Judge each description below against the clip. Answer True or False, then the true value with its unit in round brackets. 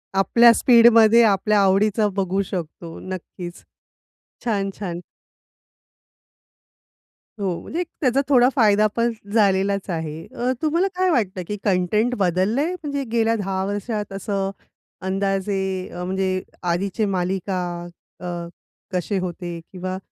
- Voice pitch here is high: True (195 Hz)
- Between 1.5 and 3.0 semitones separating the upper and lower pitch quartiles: False (3.4 semitones)